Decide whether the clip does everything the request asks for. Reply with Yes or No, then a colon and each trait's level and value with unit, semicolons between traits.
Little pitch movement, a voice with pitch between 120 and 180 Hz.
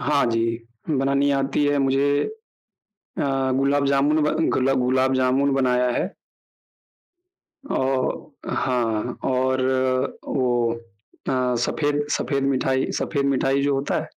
Yes: narrow, 1.5 semitones; low, 135 Hz